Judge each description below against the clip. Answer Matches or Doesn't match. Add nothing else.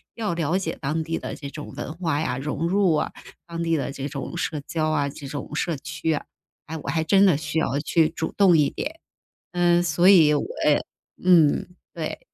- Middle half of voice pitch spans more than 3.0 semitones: Doesn't match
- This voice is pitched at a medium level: Matches